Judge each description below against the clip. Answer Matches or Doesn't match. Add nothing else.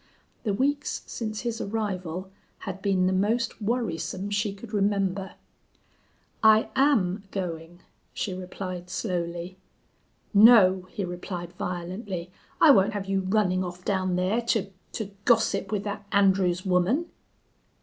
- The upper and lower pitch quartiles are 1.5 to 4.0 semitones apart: Matches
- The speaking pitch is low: Doesn't match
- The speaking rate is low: Matches